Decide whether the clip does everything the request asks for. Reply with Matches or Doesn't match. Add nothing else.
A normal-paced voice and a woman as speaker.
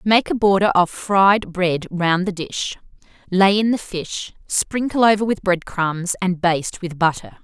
Matches